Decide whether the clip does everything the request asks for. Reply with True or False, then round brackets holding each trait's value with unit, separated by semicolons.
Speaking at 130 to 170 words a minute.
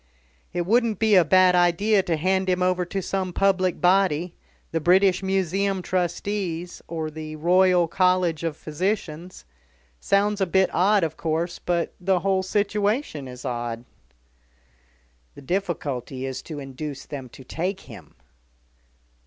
True (140 wpm)